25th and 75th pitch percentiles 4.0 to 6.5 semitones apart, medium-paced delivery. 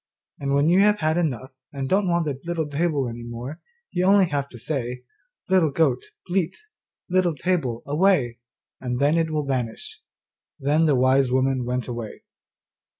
Yes: average, 5.0 semitones; average, 165 wpm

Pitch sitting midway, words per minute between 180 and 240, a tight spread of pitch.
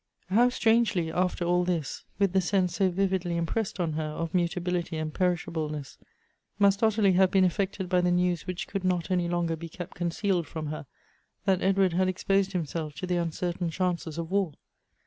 Yes: medium, 180 Hz; average, 185 wpm; narrow, 2.2 semitones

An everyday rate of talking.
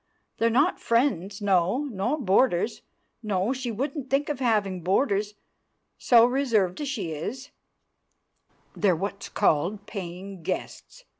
No: slow, 125 wpm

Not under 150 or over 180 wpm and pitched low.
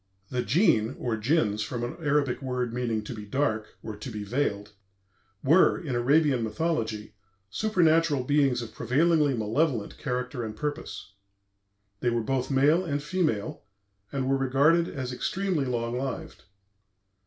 No: average, 140 wpm; low, 130 Hz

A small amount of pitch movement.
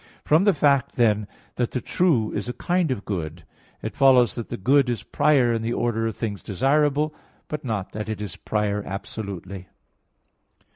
No: average, 5.1 semitones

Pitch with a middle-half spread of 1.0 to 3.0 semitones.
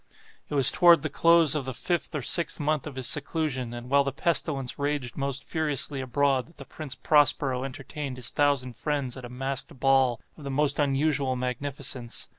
Yes: narrow, 2.4 semitones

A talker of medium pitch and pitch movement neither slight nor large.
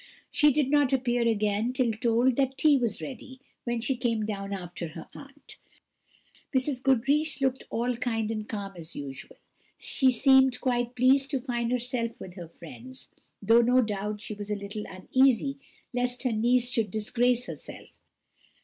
No: high, 240 Hz; average, 3.5 semitones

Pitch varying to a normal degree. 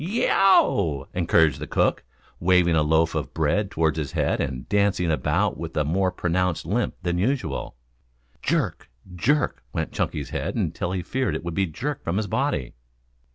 Yes: average, 4.2 semitones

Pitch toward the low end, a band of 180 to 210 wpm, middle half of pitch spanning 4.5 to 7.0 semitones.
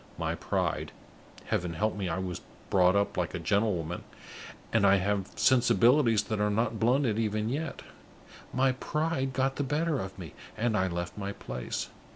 No: low, 105 Hz; average, 170 wpm; average, 5.3 semitones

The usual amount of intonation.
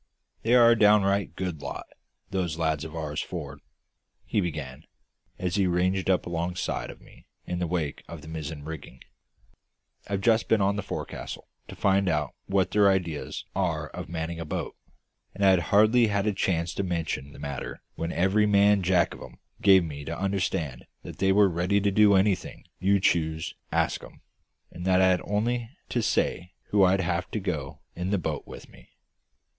Yes: average, 3.5 semitones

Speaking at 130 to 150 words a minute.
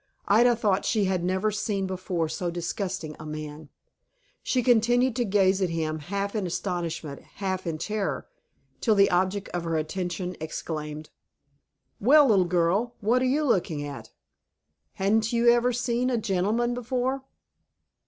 Yes: average, 145 wpm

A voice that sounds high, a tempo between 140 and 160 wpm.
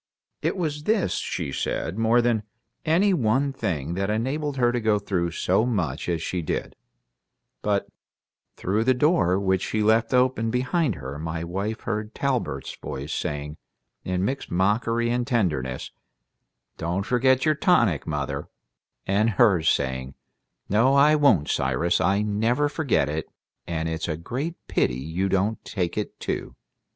No: low, 105 Hz; average, 150 wpm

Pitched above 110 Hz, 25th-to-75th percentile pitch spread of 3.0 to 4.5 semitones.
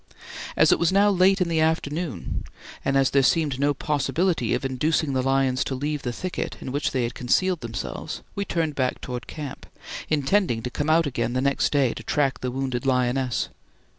Yes: medium, 140 Hz; average, 3.8 semitones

